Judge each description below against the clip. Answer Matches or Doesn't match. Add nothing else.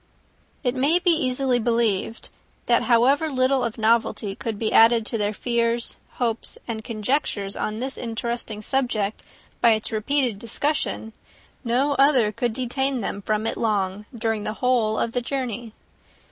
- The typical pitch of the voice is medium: Doesn't match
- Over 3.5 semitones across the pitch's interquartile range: Doesn't match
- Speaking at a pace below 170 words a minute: Matches